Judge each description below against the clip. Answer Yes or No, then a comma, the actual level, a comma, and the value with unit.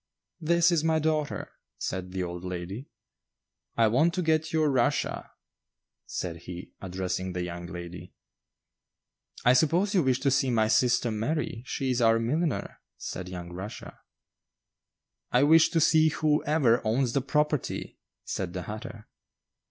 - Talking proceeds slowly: No, average, 145 wpm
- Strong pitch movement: Yes, wide, 8.8 semitones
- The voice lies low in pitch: Yes, low, 125 Hz